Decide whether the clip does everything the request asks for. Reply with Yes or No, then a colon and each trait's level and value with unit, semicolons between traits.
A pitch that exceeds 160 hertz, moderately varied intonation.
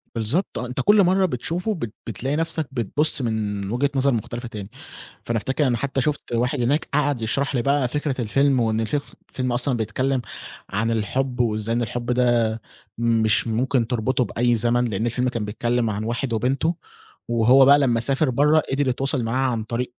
No: low, 125 Hz; average, 3.1 semitones